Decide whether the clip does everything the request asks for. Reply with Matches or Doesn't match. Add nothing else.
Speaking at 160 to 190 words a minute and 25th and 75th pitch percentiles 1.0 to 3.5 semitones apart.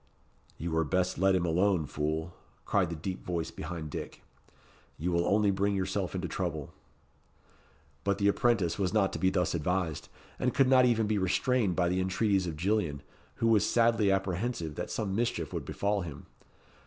Matches